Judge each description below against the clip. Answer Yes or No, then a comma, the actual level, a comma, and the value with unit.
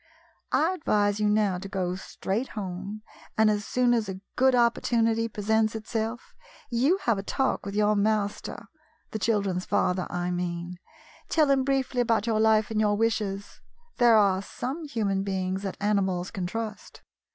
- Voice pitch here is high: Yes, high, 215 Hz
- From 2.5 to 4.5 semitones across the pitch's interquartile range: Yes, average, 2.9 semitones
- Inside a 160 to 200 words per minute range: Yes, average, 165 wpm